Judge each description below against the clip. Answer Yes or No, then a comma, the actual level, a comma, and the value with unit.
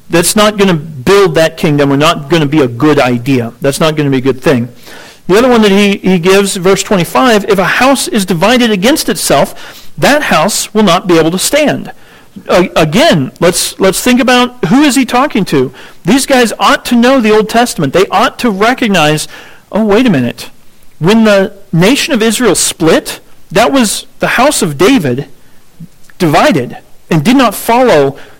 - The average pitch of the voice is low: No, high, 195 Hz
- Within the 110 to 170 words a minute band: No, average, 200 wpm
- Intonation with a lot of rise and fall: Yes, wide, 6.7 semitones